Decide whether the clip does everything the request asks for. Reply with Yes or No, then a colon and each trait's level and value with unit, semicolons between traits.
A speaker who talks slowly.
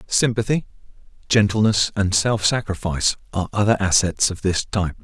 Yes: slow, 130 wpm